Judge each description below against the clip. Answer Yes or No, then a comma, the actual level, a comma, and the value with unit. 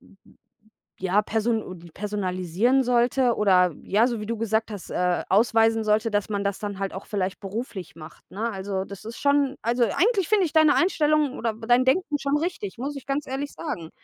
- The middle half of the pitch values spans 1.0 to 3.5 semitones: No, average, 5.3 semitones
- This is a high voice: Yes, high, 225 Hz